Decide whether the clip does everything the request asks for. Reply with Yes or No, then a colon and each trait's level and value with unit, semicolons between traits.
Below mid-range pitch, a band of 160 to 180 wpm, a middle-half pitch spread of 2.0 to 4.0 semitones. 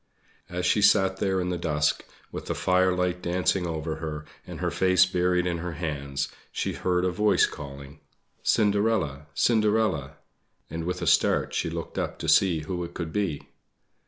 Yes: very low, 90 Hz; average, 170 wpm; average, 3.0 semitones